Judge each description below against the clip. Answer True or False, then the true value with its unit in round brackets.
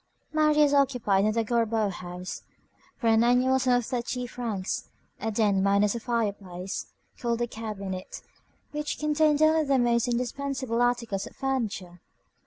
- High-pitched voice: True (235 Hz)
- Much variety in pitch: False (4.2 semitones)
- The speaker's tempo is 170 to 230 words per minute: False (145 wpm)